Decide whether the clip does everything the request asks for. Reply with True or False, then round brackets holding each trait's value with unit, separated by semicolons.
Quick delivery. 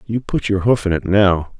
True (265 wpm)